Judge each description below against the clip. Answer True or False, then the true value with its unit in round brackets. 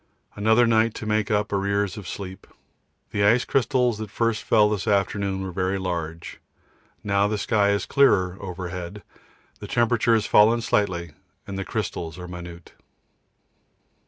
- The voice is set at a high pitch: False (100 Hz)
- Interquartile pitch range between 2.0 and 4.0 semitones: True (2.9 semitones)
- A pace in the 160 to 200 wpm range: False (150 wpm)